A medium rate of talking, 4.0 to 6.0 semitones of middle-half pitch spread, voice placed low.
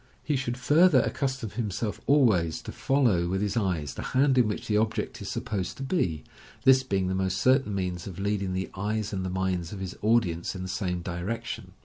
No: fast, 210 wpm; average, 4.6 semitones; low, 100 Hz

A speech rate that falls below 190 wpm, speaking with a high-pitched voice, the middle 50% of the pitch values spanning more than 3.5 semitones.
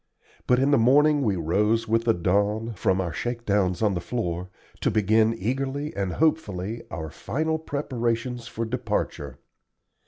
No: average, 150 wpm; low, 115 Hz; average, 4.5 semitones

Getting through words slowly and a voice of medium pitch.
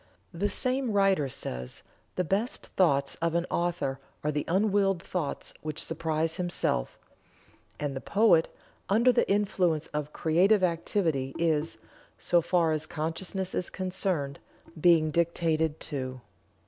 Yes: slow, 130 wpm; medium, 170 Hz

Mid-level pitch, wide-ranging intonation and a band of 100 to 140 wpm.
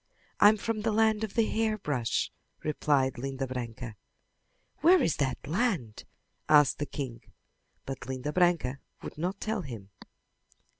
Yes: medium, 150 Hz; wide, 8.5 semitones; slow, 135 wpm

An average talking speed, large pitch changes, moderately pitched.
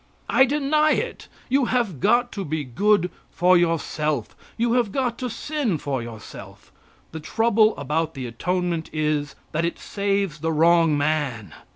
Yes: average, 155 wpm; wide, 7.2 semitones; medium, 175 Hz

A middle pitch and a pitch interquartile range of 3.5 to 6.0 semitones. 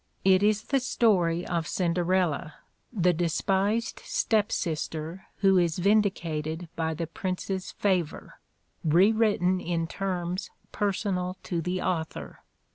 No: medium, 180 Hz; average, 3.0 semitones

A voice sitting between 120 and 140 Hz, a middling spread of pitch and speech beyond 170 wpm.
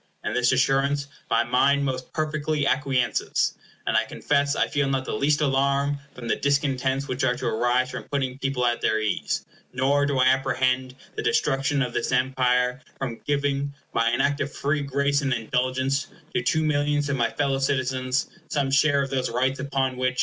No: low, 135 Hz; narrow, 1.8 semitones; average, 185 wpm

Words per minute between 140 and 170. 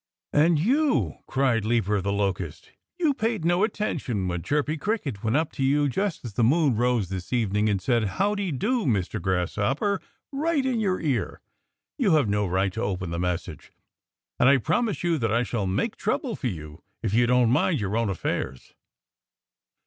No: average, 185 wpm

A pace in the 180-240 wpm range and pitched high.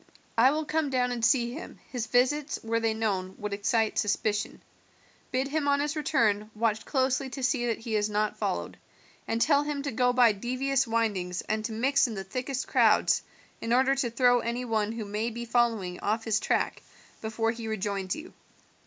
Yes: average, 195 wpm; high, 235 Hz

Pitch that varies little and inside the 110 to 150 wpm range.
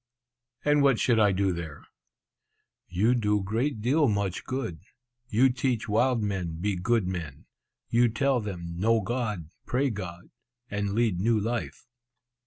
No: average, 4.4 semitones; average, 145 wpm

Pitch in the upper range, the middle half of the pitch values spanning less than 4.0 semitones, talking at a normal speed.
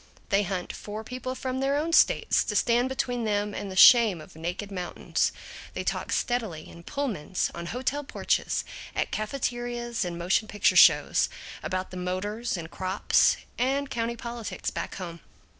No: high, 215 Hz; average, 4.9 semitones; average, 160 wpm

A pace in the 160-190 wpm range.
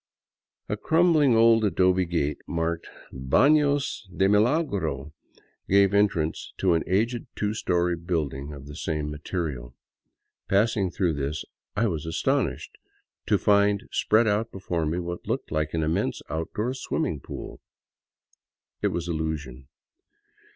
No: slow, 135 wpm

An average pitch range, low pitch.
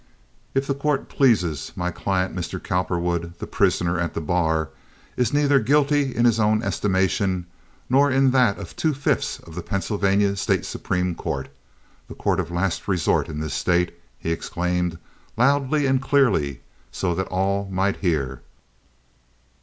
No: wide, 6.5 semitones; very low, 95 Hz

